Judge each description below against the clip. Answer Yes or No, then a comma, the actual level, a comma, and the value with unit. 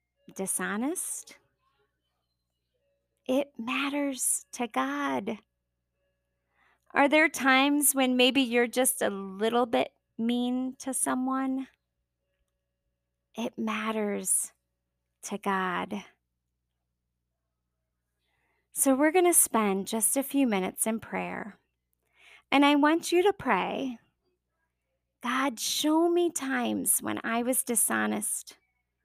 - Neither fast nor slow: No, slow, 95 wpm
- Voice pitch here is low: No, high, 220 Hz